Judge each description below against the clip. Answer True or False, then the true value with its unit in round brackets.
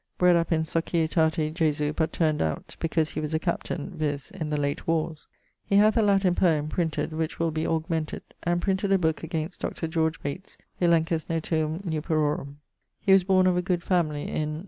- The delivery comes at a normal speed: True (190 wpm)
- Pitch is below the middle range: False (160 Hz)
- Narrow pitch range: True (2.3 semitones)